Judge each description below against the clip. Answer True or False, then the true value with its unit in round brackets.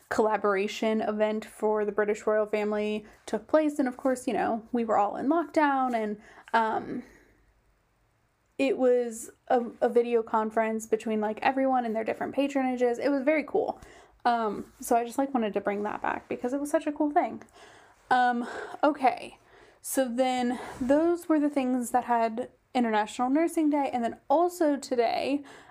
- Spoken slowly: False (170 wpm)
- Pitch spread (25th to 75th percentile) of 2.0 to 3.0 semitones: False (4.2 semitones)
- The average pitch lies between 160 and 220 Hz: False (245 Hz)